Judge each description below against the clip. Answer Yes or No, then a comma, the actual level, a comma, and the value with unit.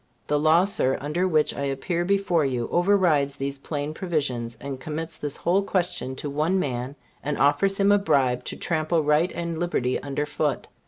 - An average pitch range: Yes, average, 3.9 semitones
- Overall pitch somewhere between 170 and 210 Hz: No, medium, 150 Hz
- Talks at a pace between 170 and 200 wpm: Yes, average, 180 wpm